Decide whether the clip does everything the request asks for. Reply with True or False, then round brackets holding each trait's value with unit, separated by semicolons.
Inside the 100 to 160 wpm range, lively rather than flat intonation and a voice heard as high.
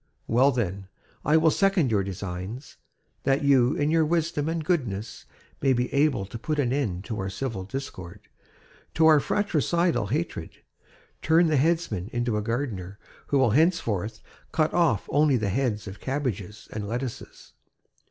False (155 wpm; 6.7 semitones; 130 Hz)